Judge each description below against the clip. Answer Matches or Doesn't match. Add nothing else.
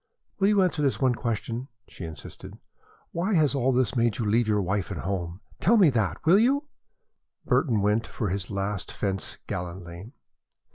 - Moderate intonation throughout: Doesn't match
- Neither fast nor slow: Matches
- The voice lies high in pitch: Doesn't match